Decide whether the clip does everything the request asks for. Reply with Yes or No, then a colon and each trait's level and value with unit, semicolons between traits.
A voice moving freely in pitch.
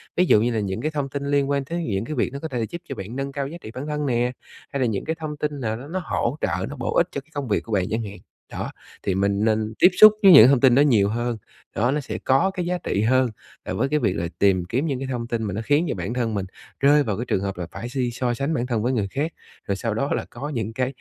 No: average, 4.6 semitones